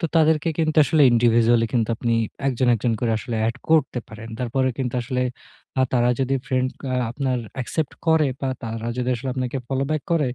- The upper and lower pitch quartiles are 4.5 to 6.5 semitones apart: No, average, 2.8 semitones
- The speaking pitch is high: No, low, 130 Hz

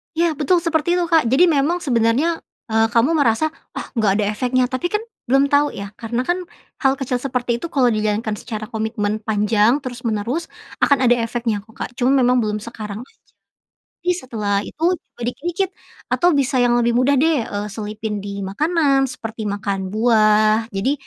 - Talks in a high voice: Yes, high, 240 Hz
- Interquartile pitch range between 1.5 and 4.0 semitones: No, average, 4.7 semitones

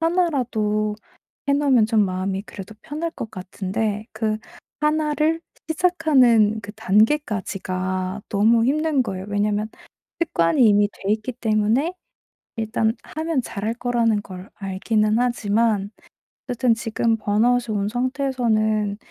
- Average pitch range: Yes, average, 3.8 semitones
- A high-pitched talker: Yes, high, 220 Hz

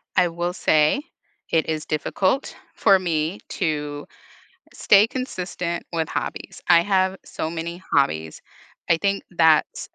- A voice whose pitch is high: No, medium, 170 Hz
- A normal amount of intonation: Yes, average, 3.1 semitones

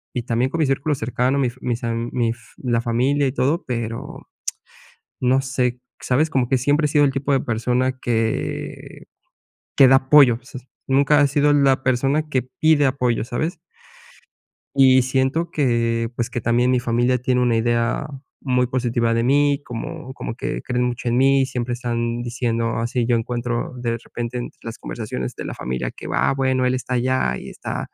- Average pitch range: No, narrow, 2.3 semitones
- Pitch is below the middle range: Yes, low, 125 Hz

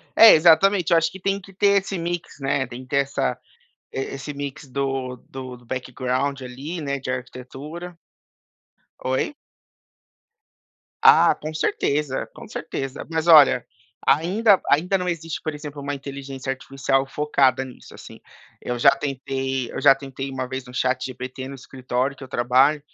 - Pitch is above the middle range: No, low, 135 Hz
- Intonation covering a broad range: No, average, 3.3 semitones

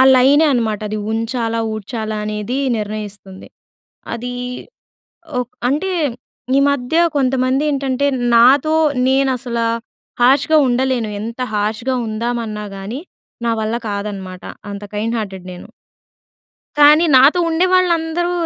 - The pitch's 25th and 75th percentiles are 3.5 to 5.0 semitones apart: Yes, average, 4.3 semitones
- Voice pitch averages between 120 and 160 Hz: No, high, 240 Hz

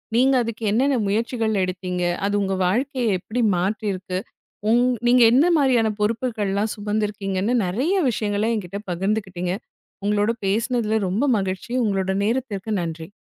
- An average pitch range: Yes, average, 3.5 semitones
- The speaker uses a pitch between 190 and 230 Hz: Yes, high, 210 Hz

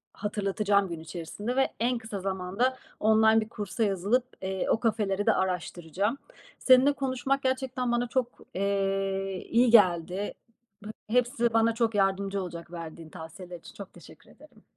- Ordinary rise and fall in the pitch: Yes, average, 3.9 semitones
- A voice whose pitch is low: No, high, 205 Hz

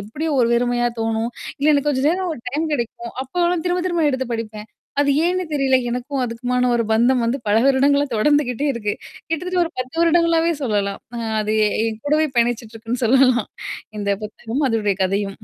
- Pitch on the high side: Yes, very high, 250 Hz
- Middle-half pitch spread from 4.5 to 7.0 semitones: Yes, average, 4.8 semitones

